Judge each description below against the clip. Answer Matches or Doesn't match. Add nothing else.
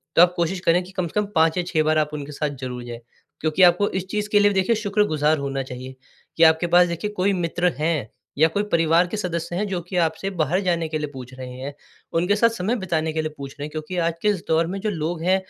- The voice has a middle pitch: Matches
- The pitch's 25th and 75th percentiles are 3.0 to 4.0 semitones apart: Matches